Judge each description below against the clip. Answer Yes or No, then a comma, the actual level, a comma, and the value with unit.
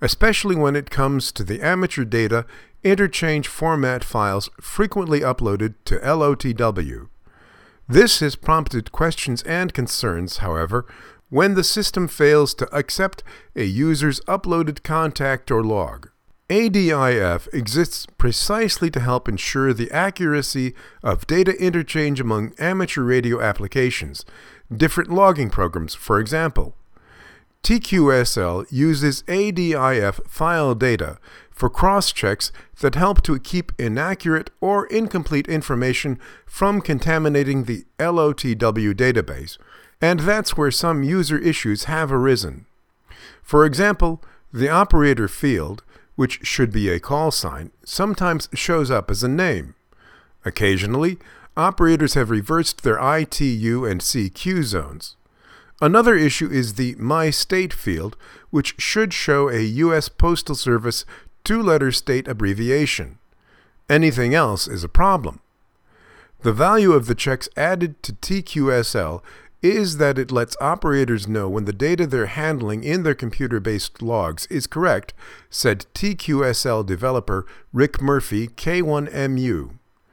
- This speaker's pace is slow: Yes, slow, 125 wpm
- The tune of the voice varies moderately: No, wide, 5.9 semitones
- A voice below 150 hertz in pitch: Yes, medium, 140 Hz